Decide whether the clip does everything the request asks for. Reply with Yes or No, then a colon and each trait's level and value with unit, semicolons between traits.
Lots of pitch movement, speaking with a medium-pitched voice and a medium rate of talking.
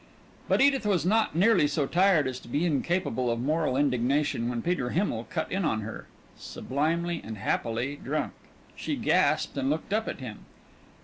Yes: wide, 5.8 semitones; medium, 150 Hz; average, 175 wpm